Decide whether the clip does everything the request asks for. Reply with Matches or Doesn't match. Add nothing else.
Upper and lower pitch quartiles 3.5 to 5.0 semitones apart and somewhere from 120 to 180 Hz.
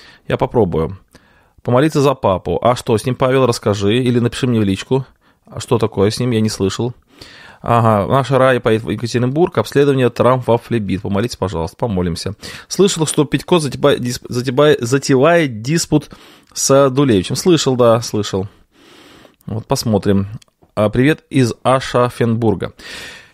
Matches